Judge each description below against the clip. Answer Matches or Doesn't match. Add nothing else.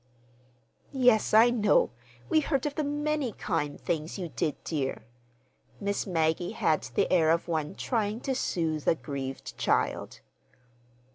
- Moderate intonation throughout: Doesn't match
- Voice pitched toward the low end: Doesn't match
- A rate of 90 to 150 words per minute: Matches